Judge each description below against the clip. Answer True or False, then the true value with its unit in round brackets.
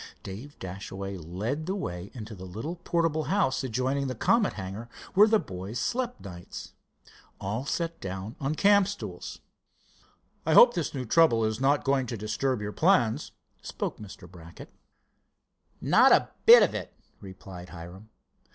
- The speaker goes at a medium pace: True (150 wpm)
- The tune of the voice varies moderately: False (8.4 semitones)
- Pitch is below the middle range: True (115 Hz)